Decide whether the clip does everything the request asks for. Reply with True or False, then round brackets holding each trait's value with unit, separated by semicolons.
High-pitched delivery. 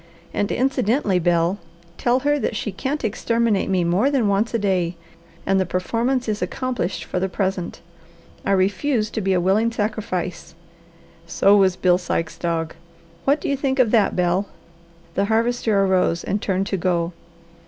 True (200 Hz)